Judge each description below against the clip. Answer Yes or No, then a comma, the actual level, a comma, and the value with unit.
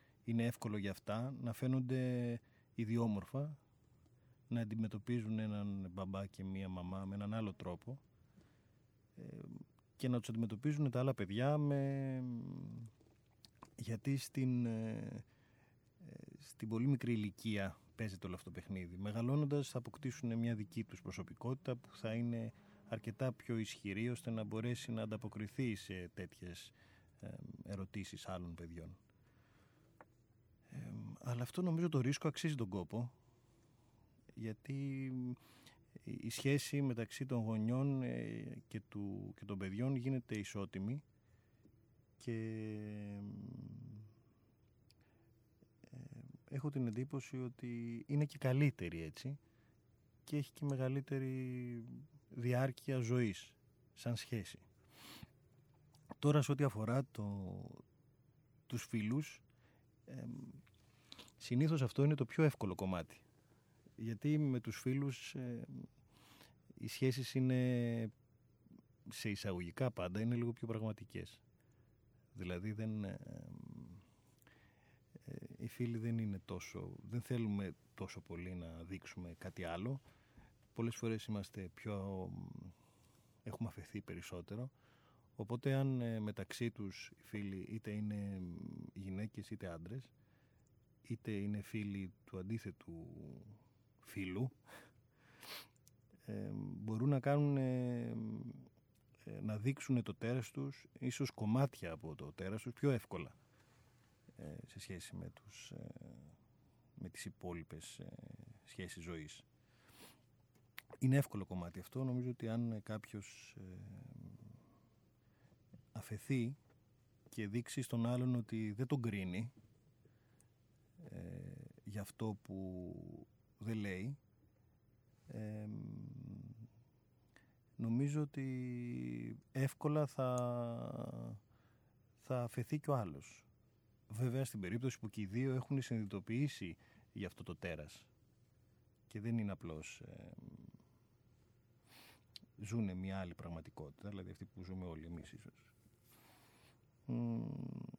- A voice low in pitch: Yes, low, 115 Hz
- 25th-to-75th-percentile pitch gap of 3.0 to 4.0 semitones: Yes, average, 3.4 semitones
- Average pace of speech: No, slow, 105 wpm